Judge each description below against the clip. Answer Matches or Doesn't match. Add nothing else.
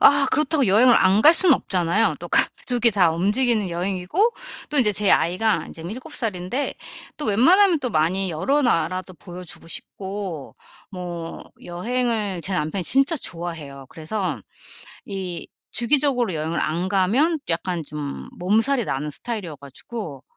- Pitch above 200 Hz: Doesn't match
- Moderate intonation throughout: Doesn't match